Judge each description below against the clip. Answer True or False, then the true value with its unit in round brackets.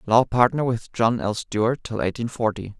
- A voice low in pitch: True (120 Hz)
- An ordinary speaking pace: True (195 wpm)